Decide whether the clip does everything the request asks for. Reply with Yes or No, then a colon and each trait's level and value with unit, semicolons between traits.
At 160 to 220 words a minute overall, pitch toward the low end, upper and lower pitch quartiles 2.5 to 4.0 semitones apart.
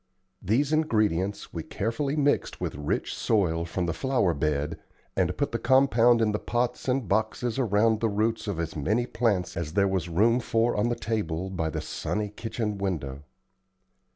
No: average, 175 wpm; low, 105 Hz; average, 5.1 semitones